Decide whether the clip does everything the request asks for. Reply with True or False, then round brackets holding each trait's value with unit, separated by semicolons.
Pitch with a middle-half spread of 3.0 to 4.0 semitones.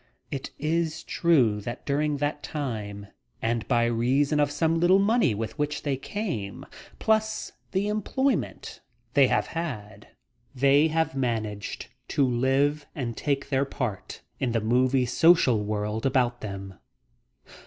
False (5.1 semitones)